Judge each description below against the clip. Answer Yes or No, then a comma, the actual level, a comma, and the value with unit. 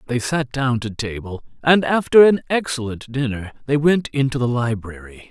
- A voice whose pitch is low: Yes, low, 130 Hz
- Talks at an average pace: Yes, average, 170 wpm